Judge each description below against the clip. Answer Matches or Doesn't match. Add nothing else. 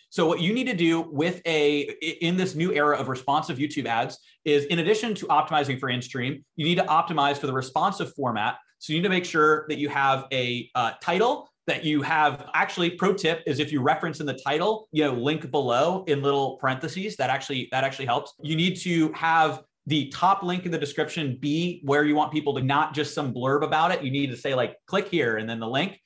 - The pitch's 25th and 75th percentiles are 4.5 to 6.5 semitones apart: Doesn't match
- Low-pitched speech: Doesn't match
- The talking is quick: Matches